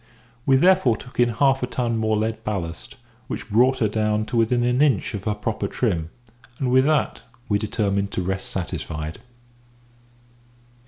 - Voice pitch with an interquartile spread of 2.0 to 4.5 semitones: Yes, average, 3.5 semitones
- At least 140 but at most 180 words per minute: Yes, average, 165 wpm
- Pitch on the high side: No, low, 110 Hz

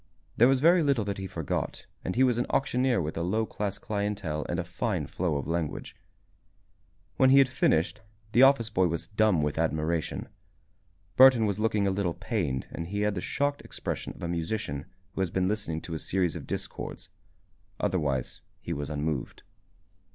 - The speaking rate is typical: Yes, average, 185 wpm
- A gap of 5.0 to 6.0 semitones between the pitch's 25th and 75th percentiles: Yes, wide, 5.4 semitones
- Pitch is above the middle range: No, very low, 95 Hz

